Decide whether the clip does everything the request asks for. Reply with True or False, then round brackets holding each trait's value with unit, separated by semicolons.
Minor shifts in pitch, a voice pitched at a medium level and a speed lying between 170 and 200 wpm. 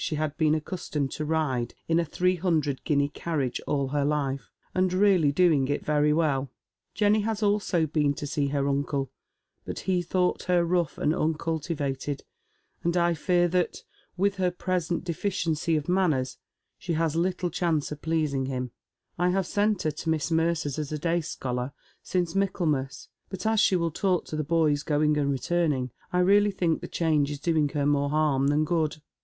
False (3.6 semitones; 160 Hz; 185 wpm)